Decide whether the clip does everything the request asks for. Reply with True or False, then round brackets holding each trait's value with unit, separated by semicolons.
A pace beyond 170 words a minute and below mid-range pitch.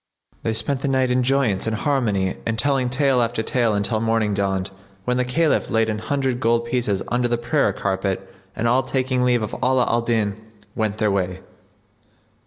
True (190 wpm; 115 Hz)